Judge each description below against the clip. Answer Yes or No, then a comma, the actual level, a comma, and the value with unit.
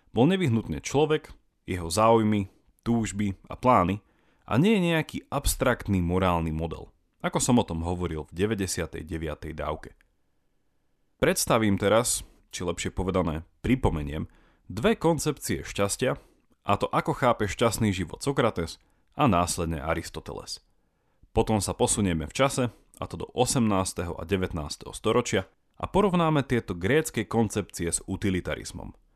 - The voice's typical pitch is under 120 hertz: Yes, low, 100 Hz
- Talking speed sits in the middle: Yes, average, 125 wpm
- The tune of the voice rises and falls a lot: Yes, wide, 6.0 semitones